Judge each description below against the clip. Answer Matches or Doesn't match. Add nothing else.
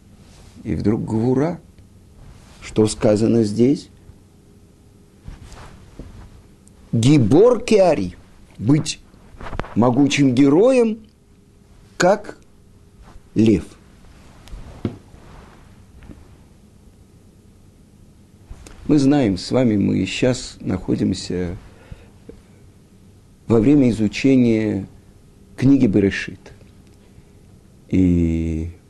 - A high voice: Doesn't match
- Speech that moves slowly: Matches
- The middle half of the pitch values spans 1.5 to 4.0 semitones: Matches